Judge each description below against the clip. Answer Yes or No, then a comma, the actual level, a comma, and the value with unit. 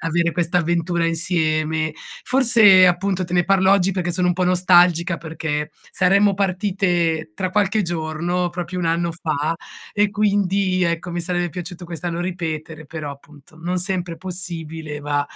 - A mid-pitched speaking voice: Yes, medium, 175 Hz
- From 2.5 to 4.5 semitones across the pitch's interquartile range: No, narrow, 2.1 semitones